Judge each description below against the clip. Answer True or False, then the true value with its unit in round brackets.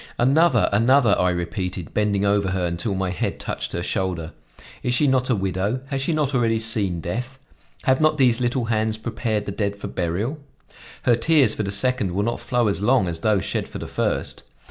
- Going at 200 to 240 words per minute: True (205 wpm)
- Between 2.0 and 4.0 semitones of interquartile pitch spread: False (4.7 semitones)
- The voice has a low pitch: True (110 Hz)